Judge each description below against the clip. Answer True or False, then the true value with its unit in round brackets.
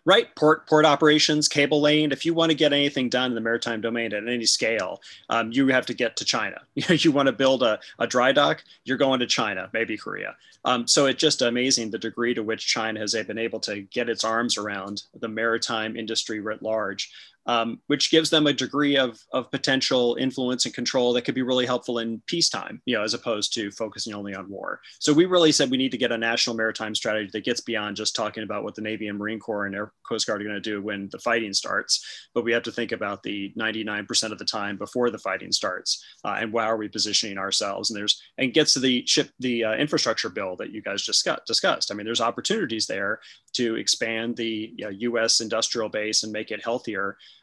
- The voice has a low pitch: True (115 Hz)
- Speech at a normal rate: False (235 wpm)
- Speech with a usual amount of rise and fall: True (3.2 semitones)